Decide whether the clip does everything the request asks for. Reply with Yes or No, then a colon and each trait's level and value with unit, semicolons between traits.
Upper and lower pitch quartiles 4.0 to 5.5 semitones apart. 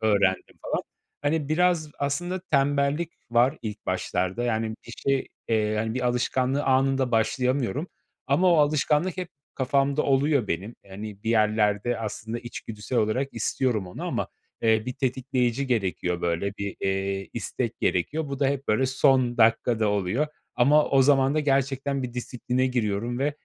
Yes: average, 4.3 semitones